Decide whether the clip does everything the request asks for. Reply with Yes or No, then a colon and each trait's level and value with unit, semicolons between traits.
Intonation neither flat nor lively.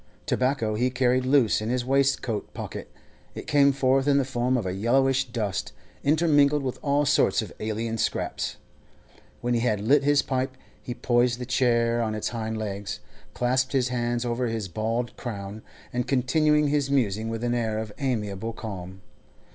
Yes: average, 3.1 semitones